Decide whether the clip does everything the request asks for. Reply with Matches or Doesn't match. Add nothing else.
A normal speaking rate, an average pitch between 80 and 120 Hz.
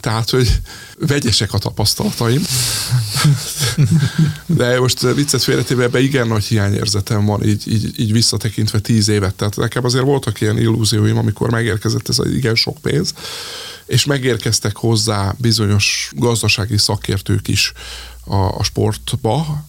Matches